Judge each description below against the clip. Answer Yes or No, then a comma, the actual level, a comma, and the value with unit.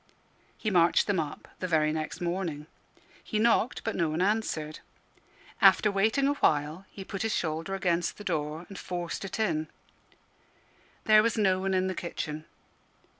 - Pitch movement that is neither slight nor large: Yes, average, 4.5 semitones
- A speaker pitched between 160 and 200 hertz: Yes, medium, 185 Hz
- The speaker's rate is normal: Yes, average, 165 wpm